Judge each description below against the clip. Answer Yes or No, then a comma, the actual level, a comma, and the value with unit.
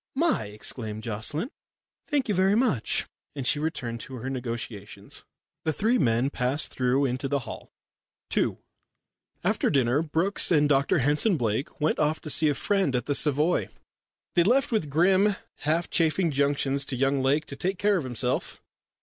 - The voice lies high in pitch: No, medium, 145 Hz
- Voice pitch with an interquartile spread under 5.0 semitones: No, average, 5.3 semitones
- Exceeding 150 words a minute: Yes, average, 170 wpm